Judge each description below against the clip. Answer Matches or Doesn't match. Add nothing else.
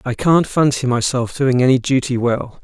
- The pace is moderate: Matches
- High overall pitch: Doesn't match